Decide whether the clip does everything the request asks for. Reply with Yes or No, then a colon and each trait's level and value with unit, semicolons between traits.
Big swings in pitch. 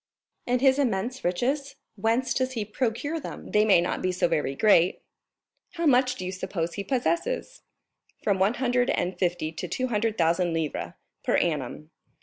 Yes: wide, 6.3 semitones